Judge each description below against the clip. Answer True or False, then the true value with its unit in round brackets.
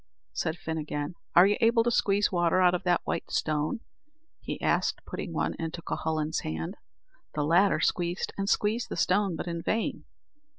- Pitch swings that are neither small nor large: True (3.9 semitones)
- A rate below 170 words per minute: False (175 wpm)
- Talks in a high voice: False (175 Hz)